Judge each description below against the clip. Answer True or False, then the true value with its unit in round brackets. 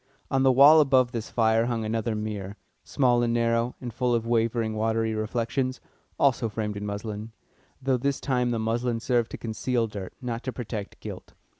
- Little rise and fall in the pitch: True (2.1 semitones)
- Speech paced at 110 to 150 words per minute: False (180 wpm)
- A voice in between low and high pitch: False (115 Hz)